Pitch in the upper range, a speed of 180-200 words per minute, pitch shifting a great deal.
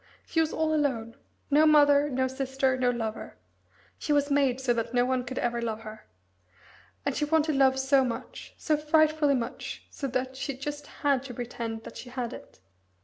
No: very high, 265 Hz; average, 190 wpm; average, 3.1 semitones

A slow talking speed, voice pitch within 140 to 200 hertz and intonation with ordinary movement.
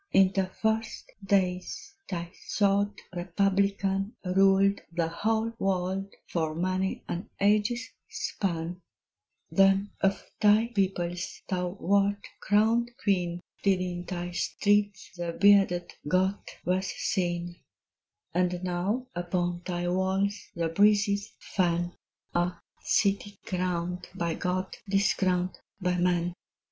No: slow, 110 wpm; medium, 185 Hz; narrow, 2.2 semitones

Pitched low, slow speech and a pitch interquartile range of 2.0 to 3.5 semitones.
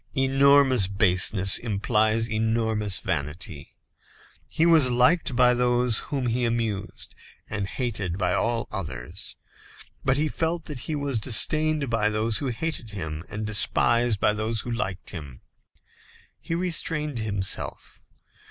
No: low, 115 Hz; slow, 130 wpm; average, 4.7 semitones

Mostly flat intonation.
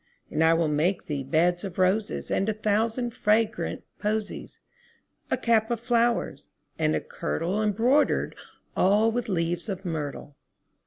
No: average, 4.7 semitones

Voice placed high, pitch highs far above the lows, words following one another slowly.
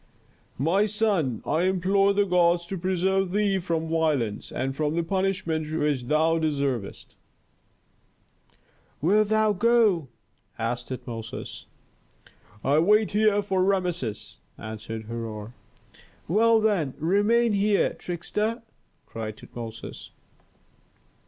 No: medium, 170 Hz; wide, 6.9 semitones; slow, 105 wpm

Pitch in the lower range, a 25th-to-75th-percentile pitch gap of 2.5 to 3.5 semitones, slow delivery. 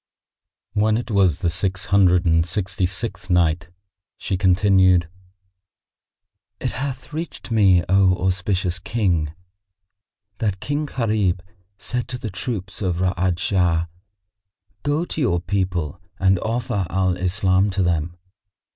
Yes: very low, 95 Hz; average, 2.9 semitones; slow, 125 wpm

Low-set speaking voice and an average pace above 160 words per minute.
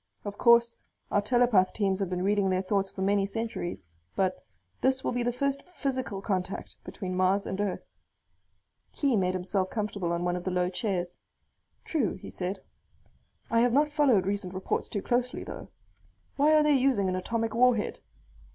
No: high, 205 Hz; average, 175 wpm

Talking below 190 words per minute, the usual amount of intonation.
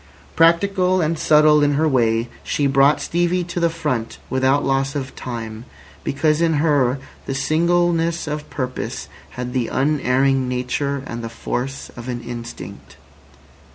Yes: average, 145 wpm; average, 4.2 semitones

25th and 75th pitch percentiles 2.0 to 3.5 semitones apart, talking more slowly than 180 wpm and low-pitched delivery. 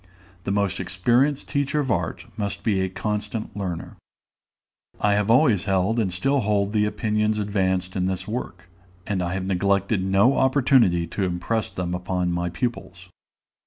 Yes: average, 3.0 semitones; average, 160 wpm; low, 100 Hz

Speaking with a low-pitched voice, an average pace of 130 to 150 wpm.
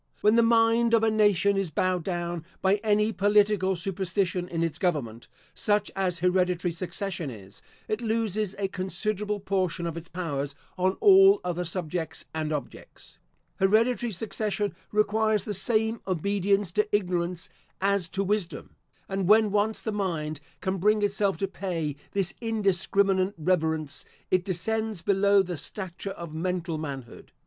No: high, 190 Hz; average, 145 wpm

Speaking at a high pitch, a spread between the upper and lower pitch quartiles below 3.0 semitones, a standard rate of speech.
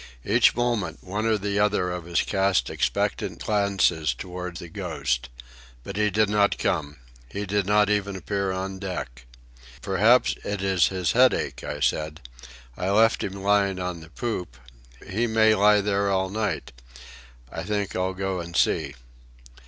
No: very low, 95 Hz; narrow, 2.5 semitones; average, 160 wpm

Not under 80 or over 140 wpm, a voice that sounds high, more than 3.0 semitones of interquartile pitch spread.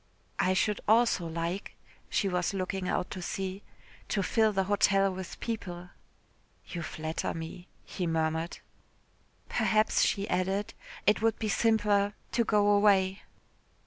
No: slow, 135 wpm; high, 195 Hz; narrow, 2.6 semitones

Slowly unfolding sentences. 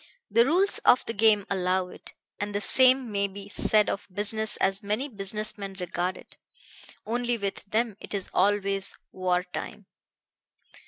No: average, 160 wpm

